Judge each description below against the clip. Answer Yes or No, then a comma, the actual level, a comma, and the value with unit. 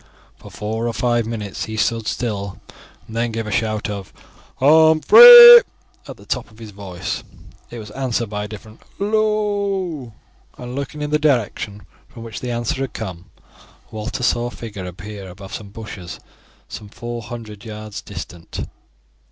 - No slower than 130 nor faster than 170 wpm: Yes, average, 160 wpm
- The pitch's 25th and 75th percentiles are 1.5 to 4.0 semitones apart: Yes, average, 3.7 semitones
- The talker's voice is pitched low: Yes, low, 115 Hz